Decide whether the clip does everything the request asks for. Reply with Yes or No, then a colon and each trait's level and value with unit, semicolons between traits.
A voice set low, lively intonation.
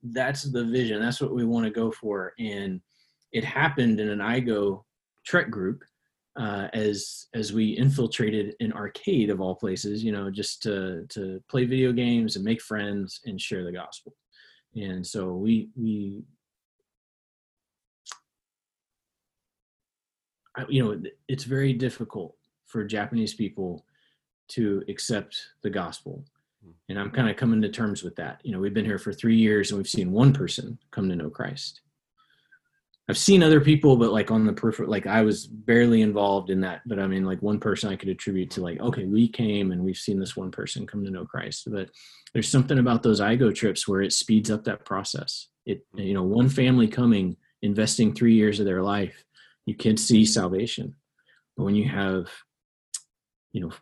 No: low, 110 Hz; average, 3.3 semitones